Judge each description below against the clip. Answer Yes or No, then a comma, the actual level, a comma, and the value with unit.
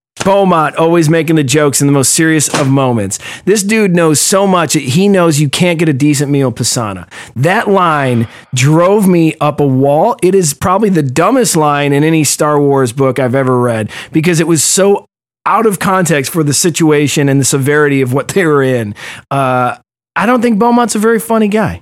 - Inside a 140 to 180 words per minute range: No, fast, 205 wpm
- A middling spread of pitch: Yes, average, 5.0 semitones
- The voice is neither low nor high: Yes, medium, 155 Hz